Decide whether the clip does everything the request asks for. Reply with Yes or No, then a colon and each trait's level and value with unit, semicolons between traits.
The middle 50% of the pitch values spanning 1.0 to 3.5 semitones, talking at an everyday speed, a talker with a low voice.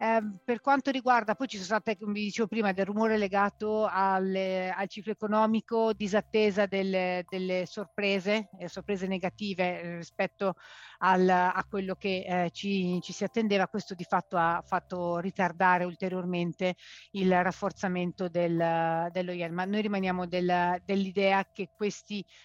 No: narrow, 2.5 semitones; average, 145 wpm; high, 190 Hz